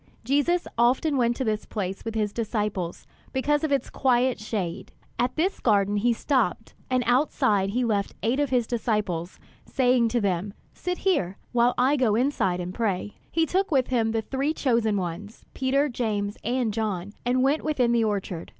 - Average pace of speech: Yes, average, 175 wpm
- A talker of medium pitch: No, high, 235 Hz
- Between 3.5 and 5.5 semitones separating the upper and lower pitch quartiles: Yes, average, 4.2 semitones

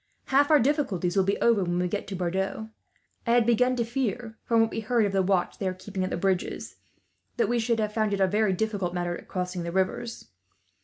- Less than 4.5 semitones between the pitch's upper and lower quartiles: Yes, average, 3.9 semitones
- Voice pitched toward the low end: No, high, 205 Hz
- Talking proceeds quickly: Yes, fast, 235 wpm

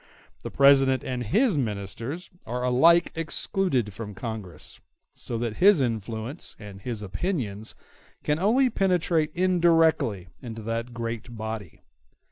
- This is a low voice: Yes, low, 125 Hz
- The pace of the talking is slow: Yes, slow, 120 wpm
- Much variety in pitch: Yes, wide, 7.0 semitones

